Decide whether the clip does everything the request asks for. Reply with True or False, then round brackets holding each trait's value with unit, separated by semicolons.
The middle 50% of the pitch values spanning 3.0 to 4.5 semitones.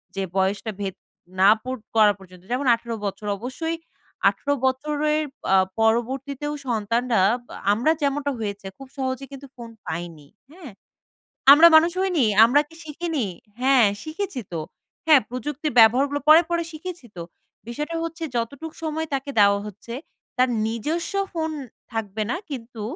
False (5.4 semitones)